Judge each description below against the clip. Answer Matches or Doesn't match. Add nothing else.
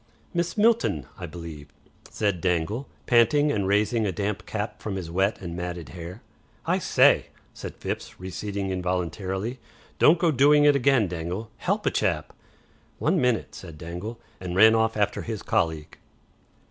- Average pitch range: Matches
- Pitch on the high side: Doesn't match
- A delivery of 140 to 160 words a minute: Matches